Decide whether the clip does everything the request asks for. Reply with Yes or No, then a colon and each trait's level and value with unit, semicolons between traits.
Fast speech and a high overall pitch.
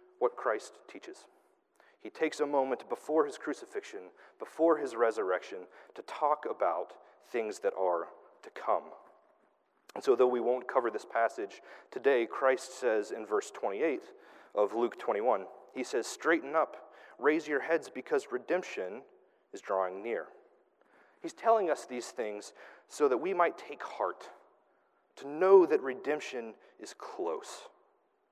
No: average, 140 wpm; very high, 395 Hz